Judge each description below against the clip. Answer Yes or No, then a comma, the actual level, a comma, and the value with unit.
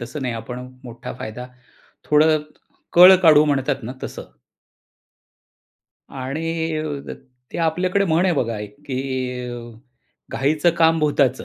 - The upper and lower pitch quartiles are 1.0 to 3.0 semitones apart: No, average, 4.3 semitones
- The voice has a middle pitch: Yes, medium, 150 Hz